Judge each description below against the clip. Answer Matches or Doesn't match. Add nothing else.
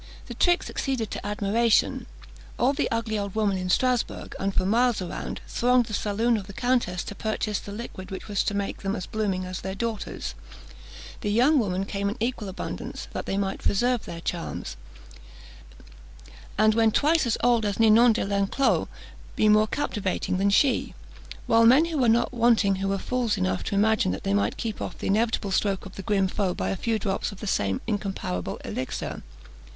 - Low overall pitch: Doesn't match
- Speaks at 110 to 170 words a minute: Doesn't match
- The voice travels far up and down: Doesn't match